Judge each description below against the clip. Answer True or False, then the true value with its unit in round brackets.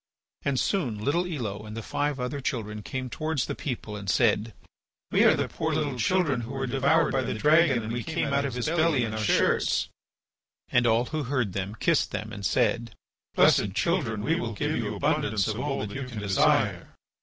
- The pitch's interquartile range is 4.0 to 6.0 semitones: True (4.8 semitones)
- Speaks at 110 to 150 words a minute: False (205 wpm)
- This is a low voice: True (125 Hz)